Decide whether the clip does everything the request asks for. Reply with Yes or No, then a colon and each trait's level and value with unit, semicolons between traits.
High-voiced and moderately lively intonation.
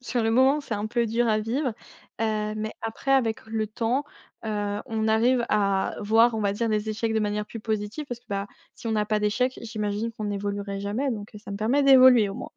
No: high, 220 Hz; narrow, 2.3 semitones